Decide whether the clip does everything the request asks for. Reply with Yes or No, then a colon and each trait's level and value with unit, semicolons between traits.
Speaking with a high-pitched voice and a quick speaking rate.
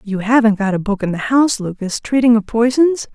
Yes: high, 225 Hz; fast, 230 wpm